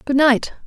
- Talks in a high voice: Yes, very high, 275 Hz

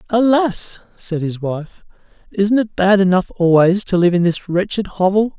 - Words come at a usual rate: Yes, average, 165 wpm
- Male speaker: Yes, male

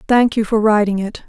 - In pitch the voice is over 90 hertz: Yes, high, 215 Hz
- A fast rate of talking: Yes, fast, 235 wpm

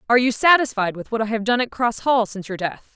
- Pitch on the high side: Yes, high, 230 Hz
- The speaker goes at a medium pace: No, fast, 285 wpm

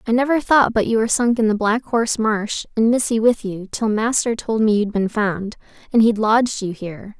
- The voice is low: No, high, 220 Hz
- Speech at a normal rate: No, fast, 225 wpm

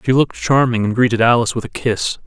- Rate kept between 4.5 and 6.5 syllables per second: No, 6.7 syllables/s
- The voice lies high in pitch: No, low, 120 Hz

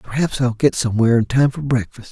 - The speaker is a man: Yes, male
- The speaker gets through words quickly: Yes, fast, 225 wpm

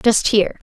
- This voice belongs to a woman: Yes, female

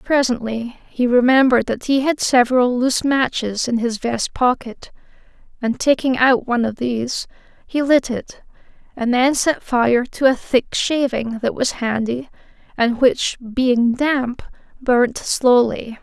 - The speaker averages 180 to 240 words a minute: No, average, 145 wpm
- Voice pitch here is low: No, very high, 250 Hz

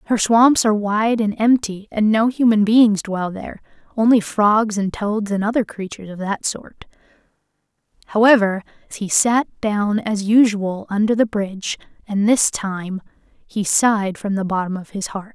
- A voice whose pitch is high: Yes, high, 210 Hz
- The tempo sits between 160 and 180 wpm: Yes, average, 165 wpm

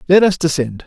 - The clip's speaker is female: No, male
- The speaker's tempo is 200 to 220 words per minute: Yes, fast, 210 wpm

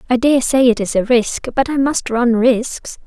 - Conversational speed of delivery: No, fast, 235 wpm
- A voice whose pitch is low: No, high, 245 Hz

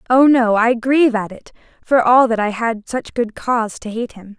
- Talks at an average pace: No, fast, 230 wpm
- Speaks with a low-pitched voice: No, high, 235 Hz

